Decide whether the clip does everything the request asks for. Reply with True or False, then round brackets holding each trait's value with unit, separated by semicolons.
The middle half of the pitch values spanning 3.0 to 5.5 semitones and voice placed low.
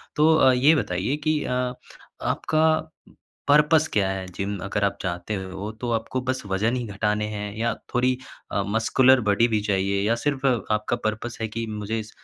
True (4.2 semitones; 110 Hz)